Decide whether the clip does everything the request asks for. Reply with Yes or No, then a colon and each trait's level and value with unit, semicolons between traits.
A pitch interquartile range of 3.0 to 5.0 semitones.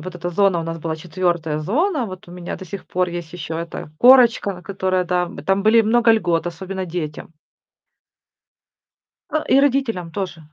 Yes: average, 3.5 semitones